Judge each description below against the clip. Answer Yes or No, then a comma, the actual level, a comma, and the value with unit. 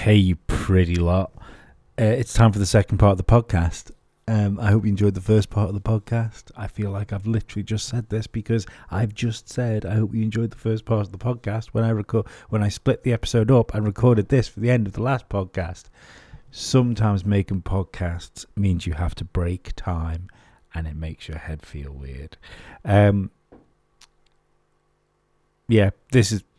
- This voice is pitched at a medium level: No, low, 105 Hz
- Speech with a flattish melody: No, average, 3.2 semitones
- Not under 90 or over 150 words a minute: No, average, 195 wpm